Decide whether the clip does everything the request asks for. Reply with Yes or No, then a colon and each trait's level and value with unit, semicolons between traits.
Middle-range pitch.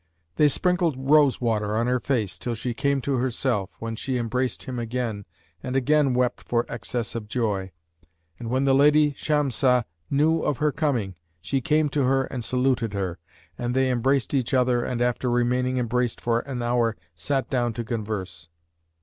No: low, 125 Hz